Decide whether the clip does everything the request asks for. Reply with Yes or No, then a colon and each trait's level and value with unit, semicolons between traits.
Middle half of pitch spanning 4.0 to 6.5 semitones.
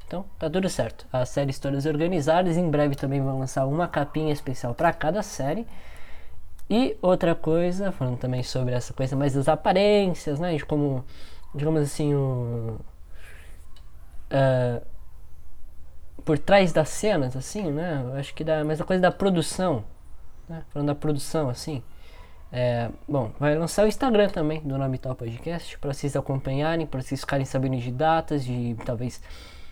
Yes: average, 4.4 semitones